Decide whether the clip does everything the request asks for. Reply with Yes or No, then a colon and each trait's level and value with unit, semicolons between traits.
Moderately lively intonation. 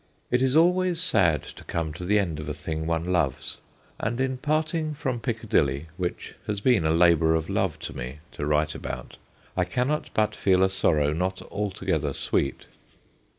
No: wide, 7.9 semitones